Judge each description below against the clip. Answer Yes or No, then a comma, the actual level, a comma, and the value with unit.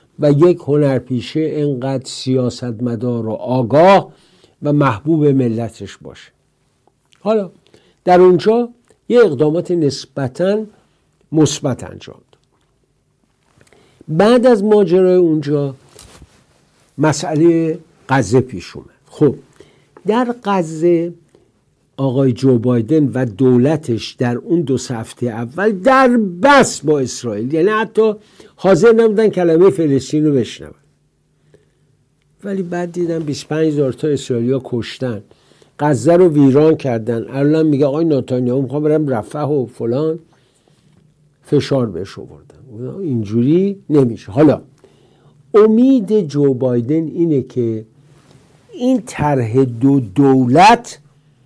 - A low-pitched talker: No, medium, 145 Hz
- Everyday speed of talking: No, slow, 105 wpm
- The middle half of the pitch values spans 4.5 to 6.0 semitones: Yes, average, 4.9 semitones